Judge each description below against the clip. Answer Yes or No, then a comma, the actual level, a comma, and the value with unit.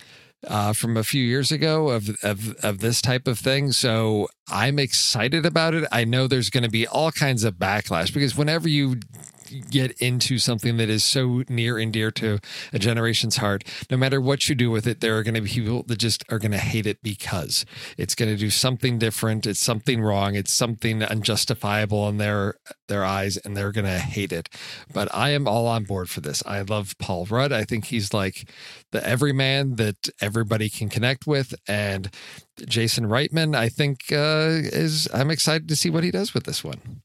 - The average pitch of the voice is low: Yes, low, 115 Hz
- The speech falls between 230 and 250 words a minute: No, fast, 205 wpm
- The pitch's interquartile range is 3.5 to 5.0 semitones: Yes, average, 4.1 semitones